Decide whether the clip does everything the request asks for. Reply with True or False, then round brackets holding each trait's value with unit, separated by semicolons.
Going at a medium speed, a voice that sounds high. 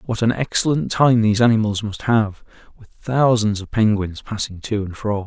False (180 wpm; 110 Hz)